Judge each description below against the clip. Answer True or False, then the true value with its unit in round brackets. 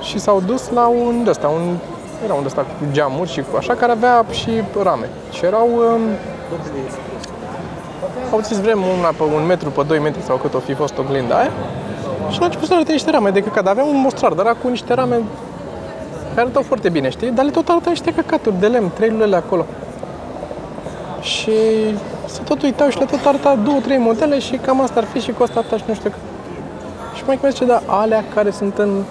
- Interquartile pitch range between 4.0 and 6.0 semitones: True (4.9 semitones)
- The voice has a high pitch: True (225 Hz)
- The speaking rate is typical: False (215 wpm)